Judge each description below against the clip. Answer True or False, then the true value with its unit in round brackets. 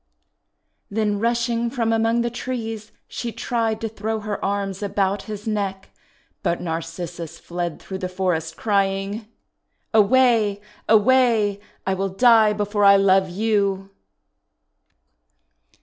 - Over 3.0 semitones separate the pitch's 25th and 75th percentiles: False (2.7 semitones)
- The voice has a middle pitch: False (205 Hz)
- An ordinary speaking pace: False (125 wpm)